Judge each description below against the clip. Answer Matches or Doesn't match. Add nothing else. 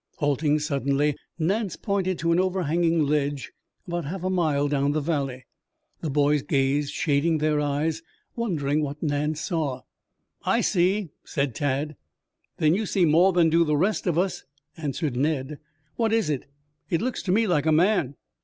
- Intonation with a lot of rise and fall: Doesn't match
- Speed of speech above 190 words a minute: Doesn't match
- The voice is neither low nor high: Matches